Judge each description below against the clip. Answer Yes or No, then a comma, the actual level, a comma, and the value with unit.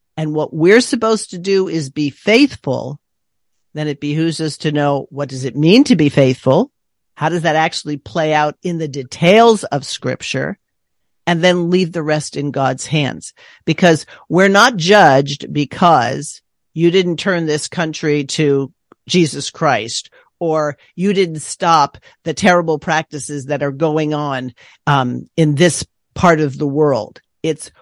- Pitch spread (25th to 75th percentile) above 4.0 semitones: No, average, 3.3 semitones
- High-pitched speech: No, medium, 155 Hz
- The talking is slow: No, average, 155 wpm